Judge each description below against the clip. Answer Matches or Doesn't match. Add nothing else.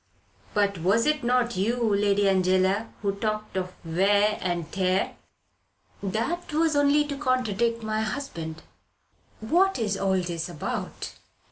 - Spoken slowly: Matches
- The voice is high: Matches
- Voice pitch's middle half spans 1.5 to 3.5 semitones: Doesn't match